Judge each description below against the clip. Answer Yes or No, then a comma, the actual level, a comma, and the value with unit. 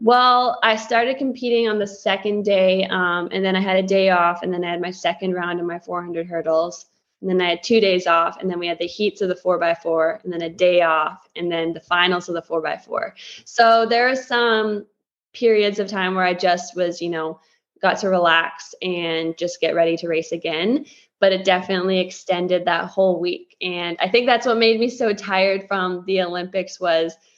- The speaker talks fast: Yes, fast, 225 wpm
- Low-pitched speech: No, medium, 180 Hz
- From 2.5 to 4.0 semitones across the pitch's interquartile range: Yes, average, 3.1 semitones